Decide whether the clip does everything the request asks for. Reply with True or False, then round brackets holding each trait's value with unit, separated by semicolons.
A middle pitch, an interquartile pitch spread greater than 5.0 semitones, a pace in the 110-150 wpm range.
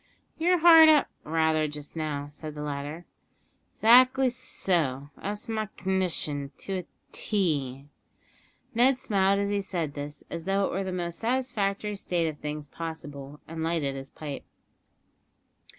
True (170 Hz; 5.6 semitones; 145 wpm)